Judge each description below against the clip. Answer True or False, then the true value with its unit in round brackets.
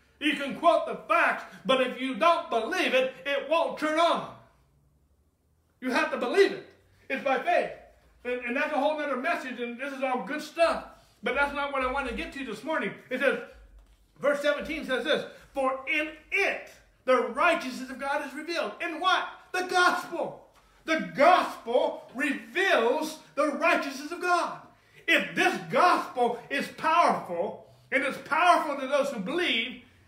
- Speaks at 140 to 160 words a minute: False (170 wpm)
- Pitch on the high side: True (285 Hz)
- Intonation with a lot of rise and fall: False (4.4 semitones)